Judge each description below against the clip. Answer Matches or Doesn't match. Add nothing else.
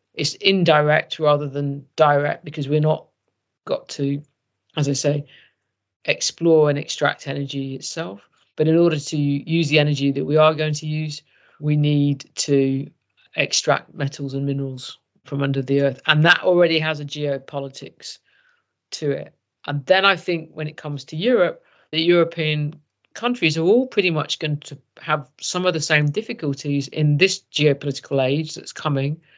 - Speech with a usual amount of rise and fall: Doesn't match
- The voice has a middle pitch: Matches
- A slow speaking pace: Doesn't match